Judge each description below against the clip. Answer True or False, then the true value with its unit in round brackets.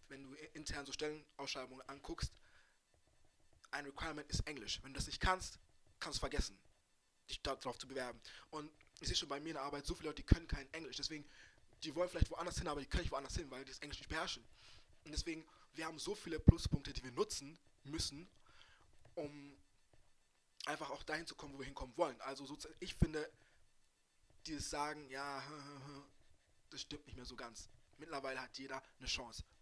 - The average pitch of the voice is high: False (140 Hz)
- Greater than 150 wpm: True (190 wpm)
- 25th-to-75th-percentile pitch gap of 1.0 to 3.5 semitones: True (2.4 semitones)